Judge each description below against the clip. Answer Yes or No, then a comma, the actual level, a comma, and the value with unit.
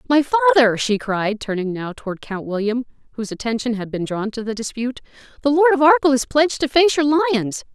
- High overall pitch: Yes, high, 230 Hz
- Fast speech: Yes, fast, 210 wpm